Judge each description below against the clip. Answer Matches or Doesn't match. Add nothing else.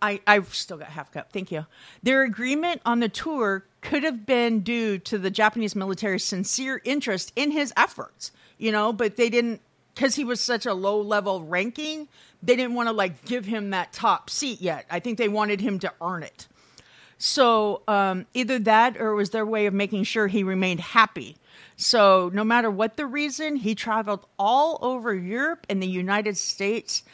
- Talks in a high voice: Matches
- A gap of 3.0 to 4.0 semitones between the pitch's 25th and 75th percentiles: Matches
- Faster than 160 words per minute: Matches